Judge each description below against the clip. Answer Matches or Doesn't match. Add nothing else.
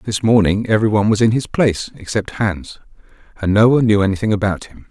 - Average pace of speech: Matches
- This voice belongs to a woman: Doesn't match